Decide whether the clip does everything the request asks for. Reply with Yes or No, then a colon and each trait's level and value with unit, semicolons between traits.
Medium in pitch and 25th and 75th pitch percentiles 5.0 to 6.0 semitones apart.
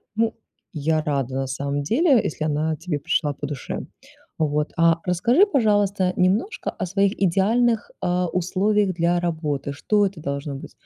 Yes: medium, 175 Hz; average, 5.3 semitones